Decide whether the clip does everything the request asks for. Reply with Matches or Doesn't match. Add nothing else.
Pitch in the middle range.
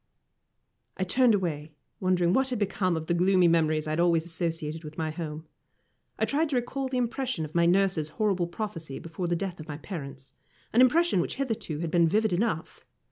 Matches